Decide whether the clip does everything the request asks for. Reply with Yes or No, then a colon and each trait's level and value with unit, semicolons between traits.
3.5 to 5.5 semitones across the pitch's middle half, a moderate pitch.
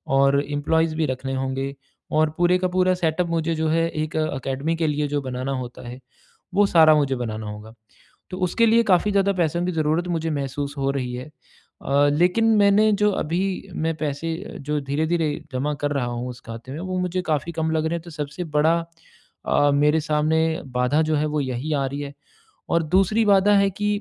Yes: average, 3.8 semitones; medium, 155 Hz